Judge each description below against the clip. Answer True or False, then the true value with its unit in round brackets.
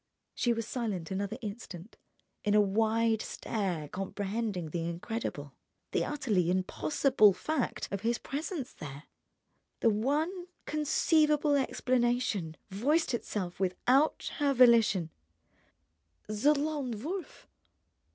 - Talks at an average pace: False (105 wpm)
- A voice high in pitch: True (225 Hz)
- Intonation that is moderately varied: False (6.3 semitones)